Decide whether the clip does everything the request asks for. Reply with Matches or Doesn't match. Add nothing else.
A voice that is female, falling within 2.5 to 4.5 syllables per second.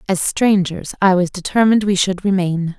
Doesn't match